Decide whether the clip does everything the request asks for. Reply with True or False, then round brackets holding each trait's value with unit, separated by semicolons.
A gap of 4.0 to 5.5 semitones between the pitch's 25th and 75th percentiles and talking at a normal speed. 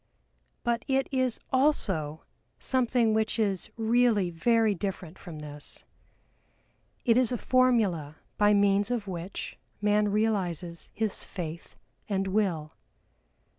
False (4.7 semitones; 115 wpm)